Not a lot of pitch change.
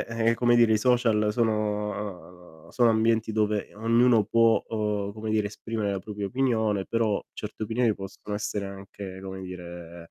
Yes: narrow, 2.3 semitones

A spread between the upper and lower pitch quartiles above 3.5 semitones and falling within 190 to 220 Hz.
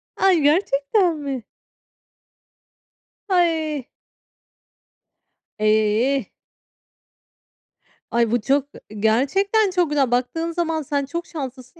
No: average, 5.1 semitones; very high, 285 Hz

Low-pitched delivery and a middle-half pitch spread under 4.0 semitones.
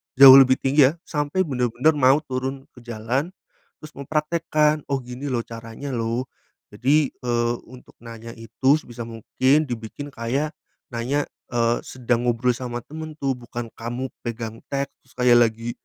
Yes: low, 125 Hz; average, 2.9 semitones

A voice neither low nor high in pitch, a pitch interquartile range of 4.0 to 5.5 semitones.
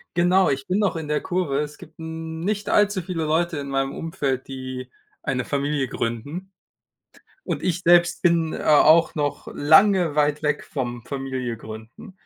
Yes: medium, 150 Hz; average, 4.3 semitones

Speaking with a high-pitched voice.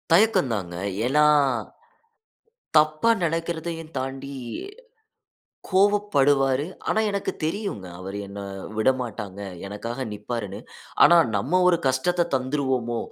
No: low, 135 Hz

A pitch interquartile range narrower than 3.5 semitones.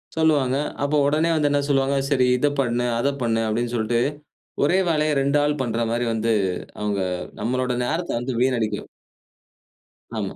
No: average, 3.8 semitones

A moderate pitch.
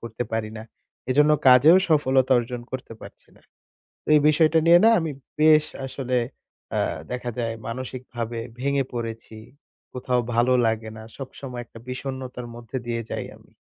No: low, 125 Hz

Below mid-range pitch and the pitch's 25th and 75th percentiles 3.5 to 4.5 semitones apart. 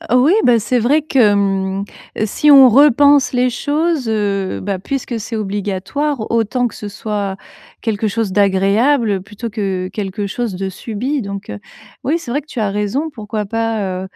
No: high, 220 Hz; average, 4.2 semitones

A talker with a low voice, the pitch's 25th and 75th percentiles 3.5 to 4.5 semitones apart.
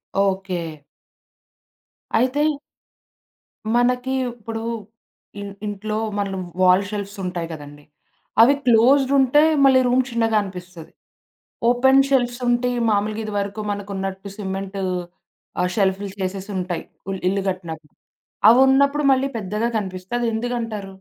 No: high, 205 Hz; average, 4.1 semitones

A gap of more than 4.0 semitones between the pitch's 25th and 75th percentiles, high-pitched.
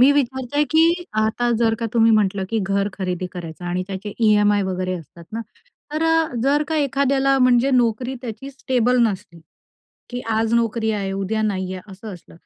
Yes: average, 5.2 semitones; high, 225 Hz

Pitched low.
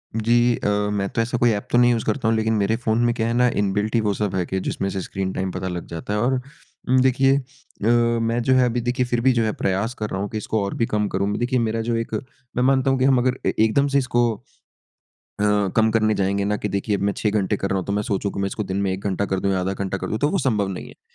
Yes: low, 110 Hz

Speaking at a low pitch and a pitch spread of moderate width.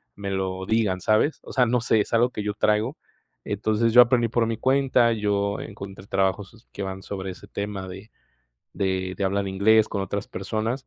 Yes: low, 105 Hz; average, 3.0 semitones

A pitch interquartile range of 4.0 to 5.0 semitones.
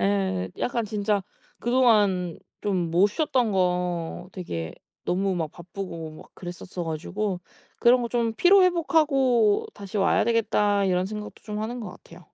Yes: average, 4.6 semitones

